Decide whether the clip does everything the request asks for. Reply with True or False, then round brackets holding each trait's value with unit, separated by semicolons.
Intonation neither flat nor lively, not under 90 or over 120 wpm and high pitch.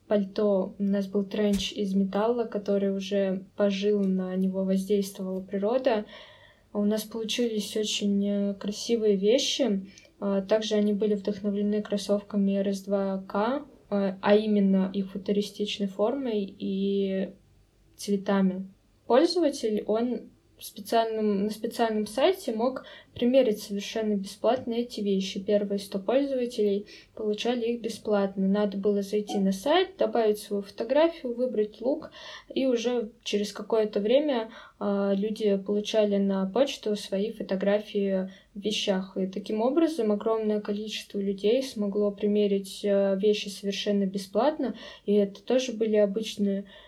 False (2.0 semitones; 115 wpm; 210 Hz)